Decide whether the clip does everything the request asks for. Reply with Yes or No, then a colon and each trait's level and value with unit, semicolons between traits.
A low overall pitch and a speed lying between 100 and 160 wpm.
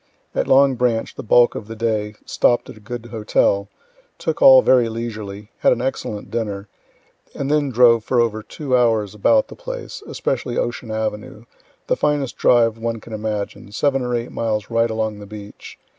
No: low, 115 Hz; average, 180 wpm